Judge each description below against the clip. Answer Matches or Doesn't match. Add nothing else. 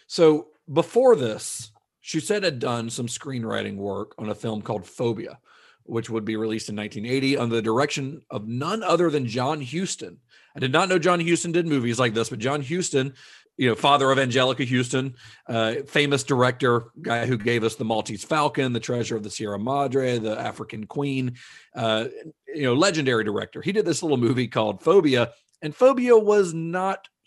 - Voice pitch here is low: Matches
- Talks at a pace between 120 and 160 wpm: Doesn't match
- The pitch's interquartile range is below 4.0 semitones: Doesn't match